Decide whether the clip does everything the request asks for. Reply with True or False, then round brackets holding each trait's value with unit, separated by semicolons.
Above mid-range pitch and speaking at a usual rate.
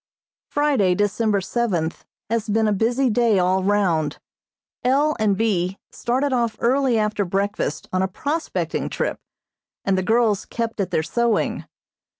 True (215 Hz; 145 wpm)